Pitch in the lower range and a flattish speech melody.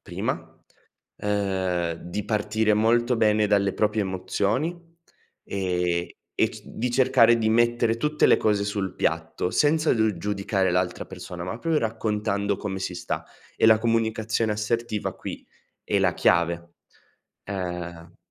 No: low, 105 Hz; average, 3.5 semitones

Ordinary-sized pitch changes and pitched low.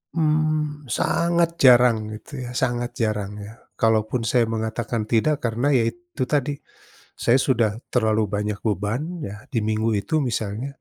Yes: average, 4.7 semitones; low, 120 Hz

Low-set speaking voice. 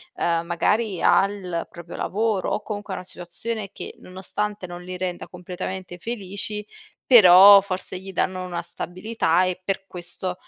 No: medium, 185 Hz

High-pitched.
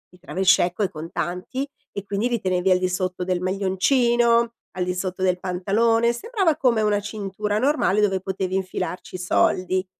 Yes: high, 195 Hz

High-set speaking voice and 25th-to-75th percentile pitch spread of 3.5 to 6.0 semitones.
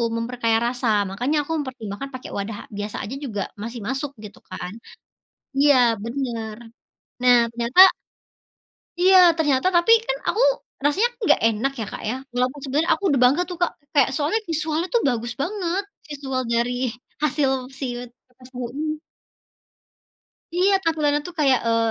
Yes: very high, 265 Hz; average, 4.5 semitones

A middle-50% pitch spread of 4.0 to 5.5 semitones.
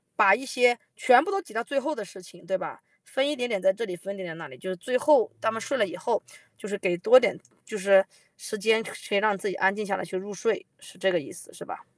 Yes: average, 4.5 semitones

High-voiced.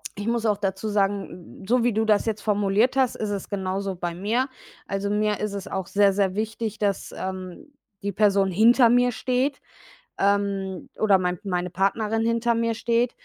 Yes: high, 205 Hz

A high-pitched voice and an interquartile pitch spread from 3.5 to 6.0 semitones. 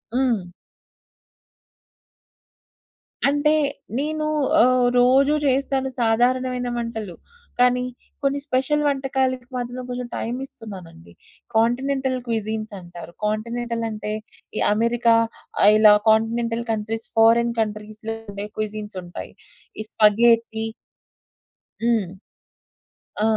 No: high, 235 Hz; average, 2.9 semitones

